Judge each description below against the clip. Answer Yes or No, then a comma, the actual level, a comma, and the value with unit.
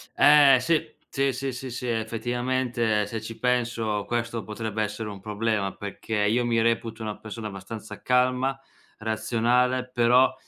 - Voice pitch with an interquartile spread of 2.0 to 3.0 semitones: Yes, narrow, 2.5 semitones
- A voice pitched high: No, low, 115 Hz